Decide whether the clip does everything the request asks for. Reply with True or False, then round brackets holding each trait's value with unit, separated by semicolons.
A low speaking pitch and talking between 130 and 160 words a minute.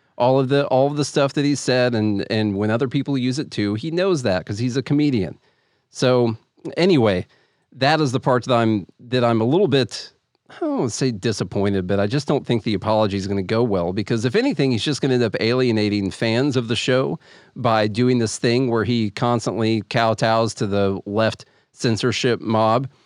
False (120 Hz; 205 wpm)